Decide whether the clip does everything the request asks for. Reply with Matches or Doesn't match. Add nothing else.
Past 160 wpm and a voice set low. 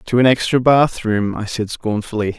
Matches